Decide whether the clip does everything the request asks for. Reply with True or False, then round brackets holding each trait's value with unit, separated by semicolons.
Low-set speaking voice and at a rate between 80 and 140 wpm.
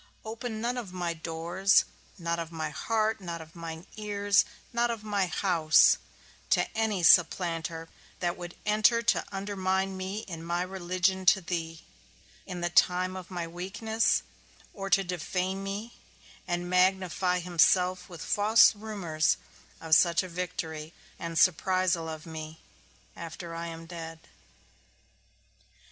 False (180 Hz; 135 wpm)